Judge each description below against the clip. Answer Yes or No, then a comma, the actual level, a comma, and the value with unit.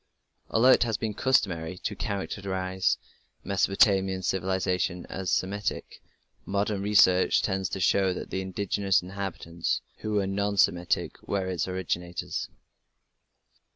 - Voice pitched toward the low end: Yes, very low, 95 Hz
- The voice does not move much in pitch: Yes, narrow, 1.6 semitones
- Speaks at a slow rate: Yes, slow, 120 wpm